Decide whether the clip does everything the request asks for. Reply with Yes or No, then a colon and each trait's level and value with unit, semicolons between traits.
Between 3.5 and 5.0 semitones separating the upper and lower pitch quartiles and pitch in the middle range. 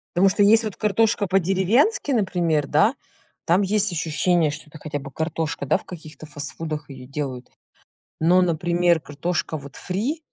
Yes: average, 4.4 semitones; medium, 170 Hz